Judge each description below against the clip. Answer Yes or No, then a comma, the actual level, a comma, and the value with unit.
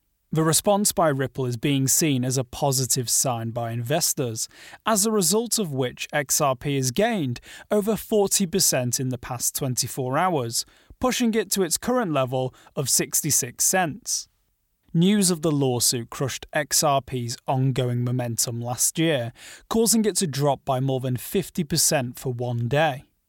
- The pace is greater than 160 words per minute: No, average, 150 wpm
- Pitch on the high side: No, medium, 140 Hz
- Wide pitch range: Yes, wide, 6.5 semitones